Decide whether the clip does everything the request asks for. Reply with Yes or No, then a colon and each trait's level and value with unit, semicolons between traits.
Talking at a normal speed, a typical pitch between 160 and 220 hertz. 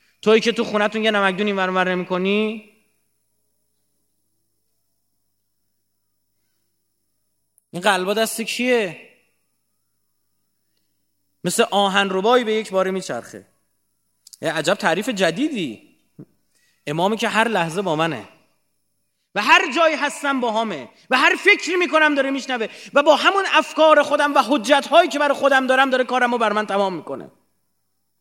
Yes: average, 130 wpm; high, 190 Hz